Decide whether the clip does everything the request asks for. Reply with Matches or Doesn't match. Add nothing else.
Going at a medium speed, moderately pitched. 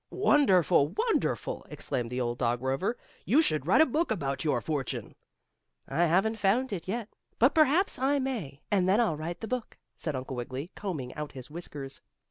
Matches